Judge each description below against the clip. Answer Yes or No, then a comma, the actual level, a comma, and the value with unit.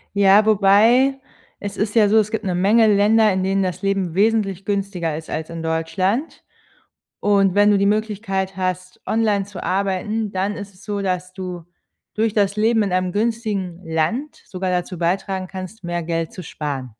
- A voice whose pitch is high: Yes, high, 195 Hz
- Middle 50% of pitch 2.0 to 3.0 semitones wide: Yes, narrow, 2.4 semitones